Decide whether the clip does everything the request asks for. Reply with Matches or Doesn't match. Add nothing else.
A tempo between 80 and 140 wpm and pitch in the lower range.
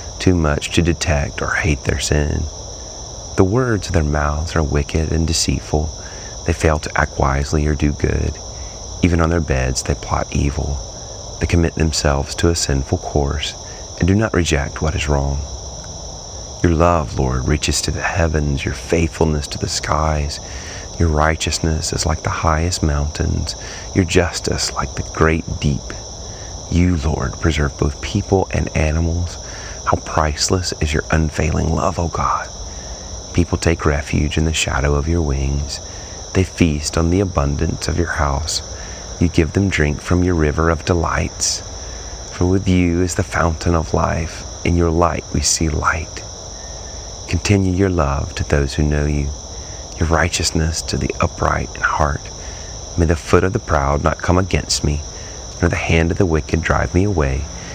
Doesn't match